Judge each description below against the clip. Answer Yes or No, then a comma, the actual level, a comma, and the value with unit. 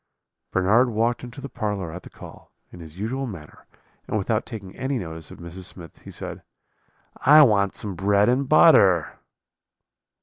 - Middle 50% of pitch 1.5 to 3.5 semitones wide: No, wide, 5.5 semitones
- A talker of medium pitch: No, low, 100 Hz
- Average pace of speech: Yes, average, 165 wpm